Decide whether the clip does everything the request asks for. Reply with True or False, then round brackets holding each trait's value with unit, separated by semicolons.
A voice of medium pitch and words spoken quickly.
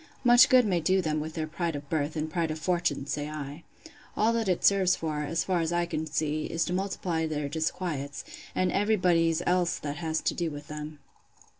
True (165 Hz; 210 wpm)